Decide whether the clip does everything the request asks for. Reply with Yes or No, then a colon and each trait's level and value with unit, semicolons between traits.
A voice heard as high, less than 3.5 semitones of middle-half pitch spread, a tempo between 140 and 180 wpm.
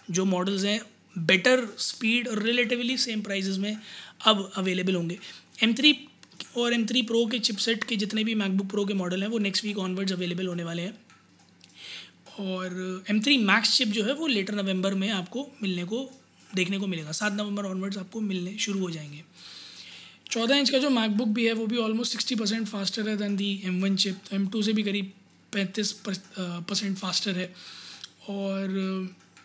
Yes: high, 200 Hz; average, 3.0 semitones; average, 175 wpm